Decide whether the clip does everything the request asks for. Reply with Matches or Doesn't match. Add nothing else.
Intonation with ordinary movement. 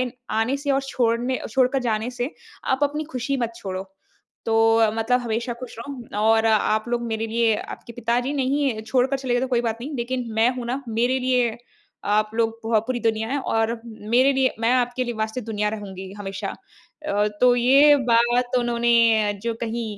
Doesn't match